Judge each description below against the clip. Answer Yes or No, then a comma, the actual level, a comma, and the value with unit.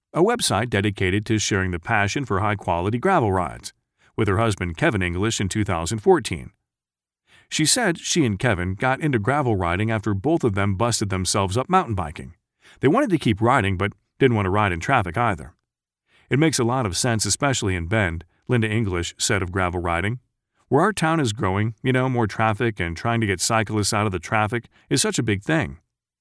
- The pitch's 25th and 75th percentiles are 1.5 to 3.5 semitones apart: No, average, 4.1 semitones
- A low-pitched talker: Yes, low, 105 Hz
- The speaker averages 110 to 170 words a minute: No, average, 200 wpm